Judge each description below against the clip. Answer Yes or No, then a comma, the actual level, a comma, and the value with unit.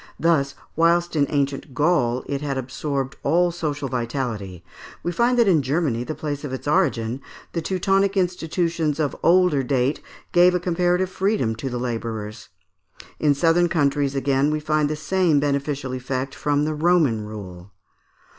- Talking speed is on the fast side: No, average, 155 wpm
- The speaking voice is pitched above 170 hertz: No, medium, 145 Hz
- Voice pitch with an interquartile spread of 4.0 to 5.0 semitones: Yes, average, 4.6 semitones